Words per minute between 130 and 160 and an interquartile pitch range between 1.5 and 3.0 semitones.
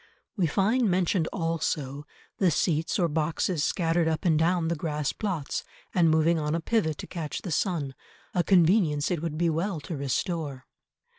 No: average, 170 wpm; average, 2.7 semitones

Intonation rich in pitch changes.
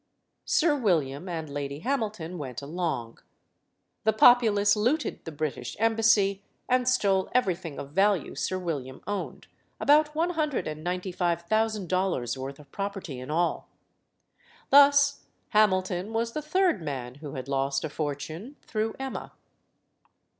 Yes: wide, 7.0 semitones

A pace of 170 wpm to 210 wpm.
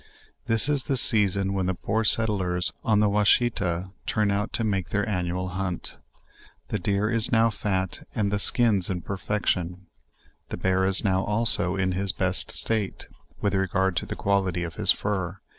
Yes: average, 175 wpm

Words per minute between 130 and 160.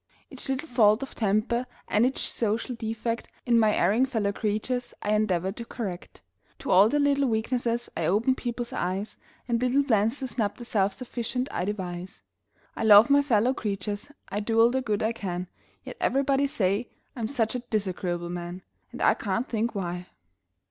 No: average, 180 wpm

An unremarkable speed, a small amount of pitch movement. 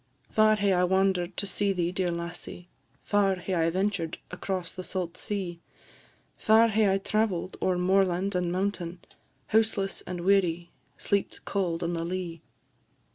Yes: average, 150 wpm; narrow, 2.2 semitones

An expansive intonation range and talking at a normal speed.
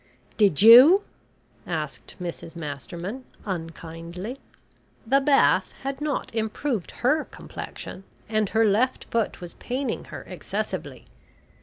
No: wide, 7.1 semitones; slow, 110 wpm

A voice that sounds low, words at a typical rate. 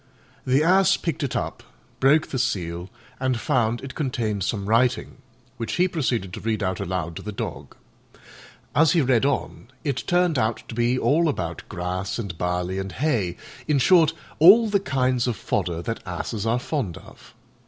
Yes: low, 120 Hz; average, 175 wpm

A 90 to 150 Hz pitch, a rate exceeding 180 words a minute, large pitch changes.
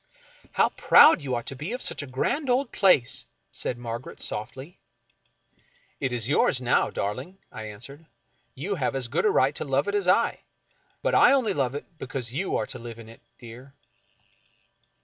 Yes: low, 135 Hz; fast, 205 wpm; wide, 7.3 semitones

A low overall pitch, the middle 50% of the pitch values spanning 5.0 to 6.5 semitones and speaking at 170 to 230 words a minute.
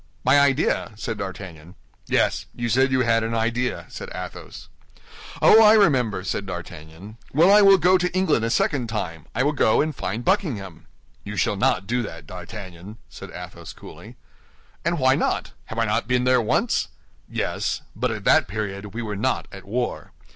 Yes: low, 115 Hz; average, 5.3 semitones; average, 180 wpm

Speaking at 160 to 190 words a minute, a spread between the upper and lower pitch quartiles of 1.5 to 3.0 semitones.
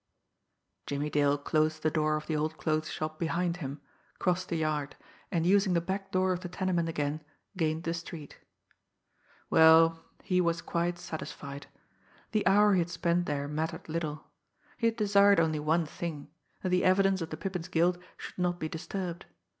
Yes: average, 175 wpm; average, 2.7 semitones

